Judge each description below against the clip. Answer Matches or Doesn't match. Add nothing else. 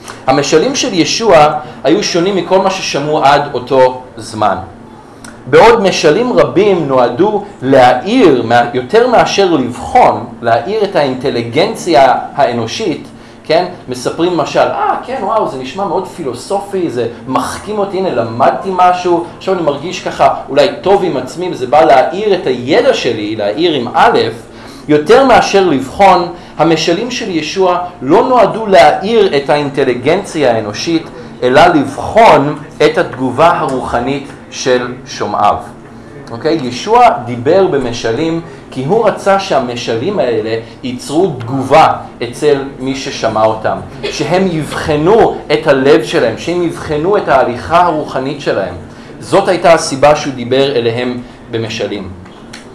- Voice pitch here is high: Doesn't match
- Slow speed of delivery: Doesn't match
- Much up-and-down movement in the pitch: Matches